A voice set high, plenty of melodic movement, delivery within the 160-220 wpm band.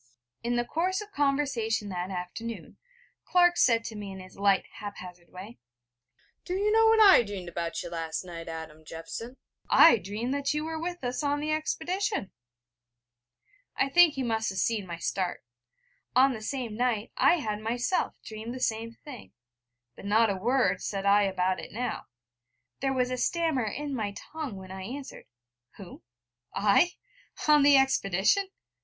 Yes: high, 230 Hz; wide, 6.6 semitones; average, 170 wpm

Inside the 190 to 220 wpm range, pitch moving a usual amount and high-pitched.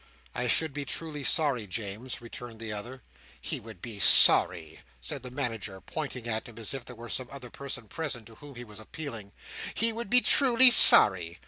No: average, 195 wpm; average, 4.7 semitones; low, 120 Hz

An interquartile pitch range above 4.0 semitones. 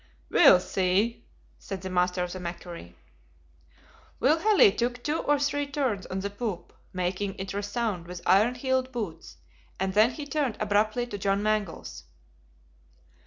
Yes: average, 5.0 semitones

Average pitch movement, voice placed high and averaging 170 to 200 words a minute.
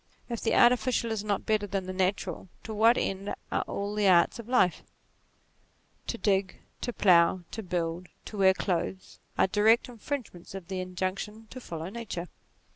Yes: average, 3.3 semitones; high, 195 Hz; average, 175 wpm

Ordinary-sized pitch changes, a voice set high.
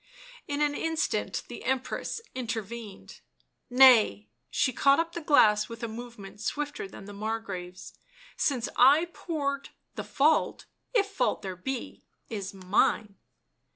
No: wide, 5.9 semitones; high, 240 Hz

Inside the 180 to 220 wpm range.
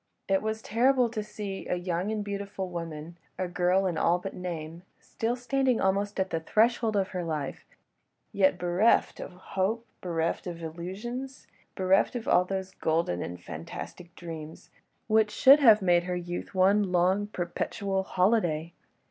No: average, 150 wpm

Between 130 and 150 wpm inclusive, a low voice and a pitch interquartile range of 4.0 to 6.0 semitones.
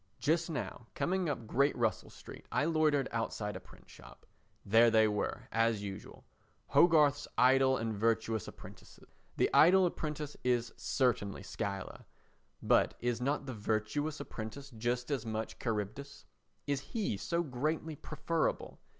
Yes: slow, 135 wpm; low, 125 Hz; average, 5.1 semitones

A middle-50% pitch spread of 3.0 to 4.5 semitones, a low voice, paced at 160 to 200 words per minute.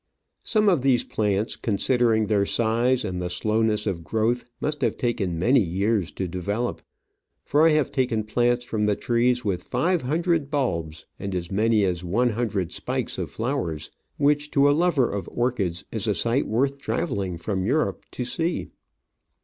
No: average, 4.9 semitones; low, 115 Hz; average, 170 wpm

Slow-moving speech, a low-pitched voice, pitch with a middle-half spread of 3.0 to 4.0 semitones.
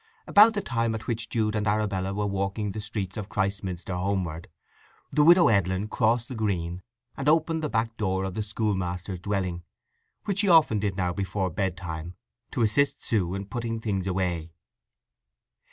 No: average, 170 wpm; low, 100 Hz; average, 3.4 semitones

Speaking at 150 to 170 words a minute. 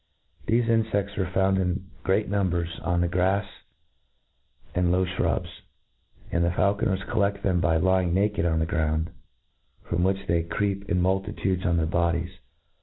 Yes: average, 160 wpm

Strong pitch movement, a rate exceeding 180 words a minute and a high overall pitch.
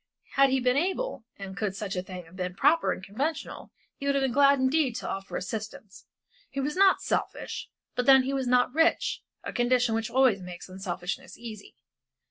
Yes: wide, 5.8 semitones; average, 195 wpm; high, 245 Hz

